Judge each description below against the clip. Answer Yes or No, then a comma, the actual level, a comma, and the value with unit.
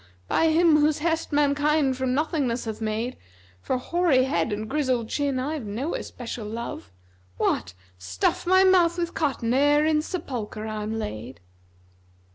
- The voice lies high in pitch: Yes, very high, 265 Hz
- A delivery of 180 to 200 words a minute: No, average, 150 wpm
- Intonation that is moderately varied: No, wide, 5.7 semitones